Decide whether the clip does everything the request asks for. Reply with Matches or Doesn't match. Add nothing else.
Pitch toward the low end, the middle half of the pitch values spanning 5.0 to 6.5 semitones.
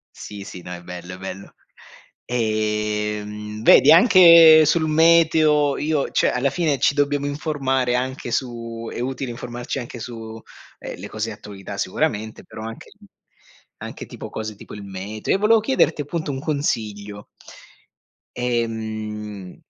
Matches